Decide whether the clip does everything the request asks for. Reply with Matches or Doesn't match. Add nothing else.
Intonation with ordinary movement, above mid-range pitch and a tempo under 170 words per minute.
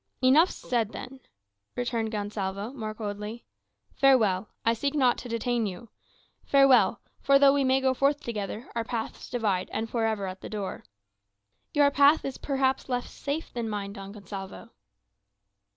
Matches